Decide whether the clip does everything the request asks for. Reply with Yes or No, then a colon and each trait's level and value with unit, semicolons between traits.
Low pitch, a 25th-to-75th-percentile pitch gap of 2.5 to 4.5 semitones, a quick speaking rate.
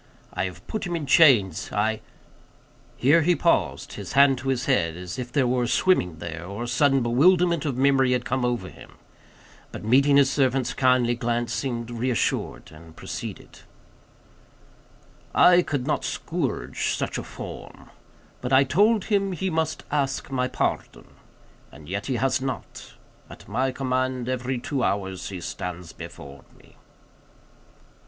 No: low, 130 Hz; average, 3.4 semitones; average, 155 wpm